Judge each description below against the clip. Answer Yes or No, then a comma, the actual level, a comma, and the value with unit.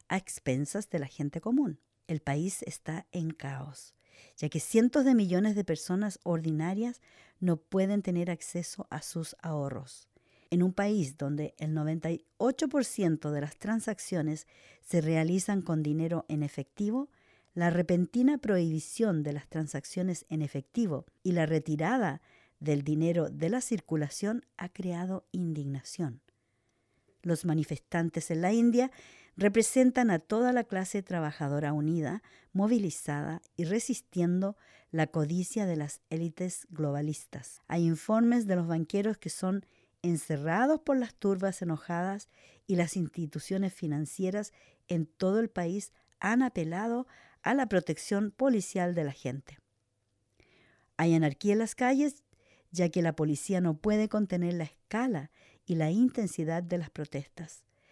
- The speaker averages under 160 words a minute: Yes, slow, 135 wpm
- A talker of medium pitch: Yes, medium, 170 Hz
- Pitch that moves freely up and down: No, average, 4.9 semitones